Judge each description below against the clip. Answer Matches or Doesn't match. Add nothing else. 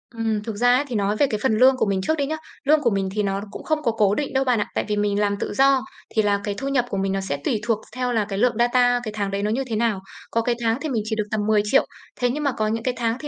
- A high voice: Matches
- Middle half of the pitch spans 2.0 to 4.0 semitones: Matches